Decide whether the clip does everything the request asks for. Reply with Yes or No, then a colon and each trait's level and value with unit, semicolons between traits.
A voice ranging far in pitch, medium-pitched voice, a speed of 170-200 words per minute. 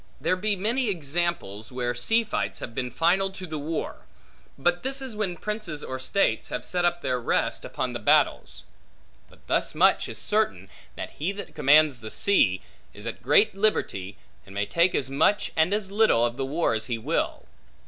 Yes: wide, 8.0 semitones; medium, 165 Hz; average, 190 wpm